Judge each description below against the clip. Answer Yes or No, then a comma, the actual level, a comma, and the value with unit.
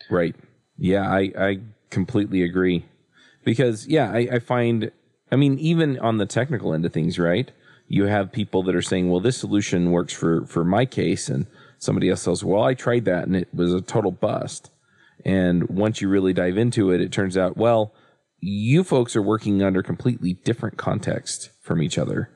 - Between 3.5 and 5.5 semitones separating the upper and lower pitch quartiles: Yes, average, 4.6 semitones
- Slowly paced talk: No, average, 190 wpm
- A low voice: Yes, low, 100 Hz